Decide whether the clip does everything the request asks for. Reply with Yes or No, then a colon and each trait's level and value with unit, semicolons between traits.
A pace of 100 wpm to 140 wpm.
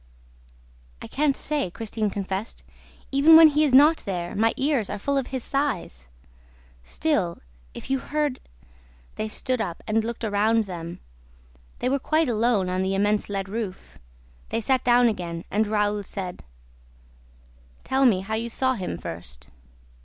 No: average, 160 wpm